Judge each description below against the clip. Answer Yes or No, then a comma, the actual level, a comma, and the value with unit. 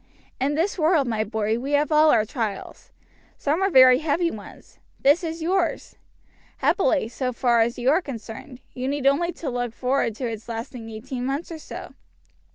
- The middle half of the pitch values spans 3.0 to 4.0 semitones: No, average, 4.9 semitones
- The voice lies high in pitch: Yes, very high, 265 Hz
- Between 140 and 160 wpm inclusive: No, average, 175 wpm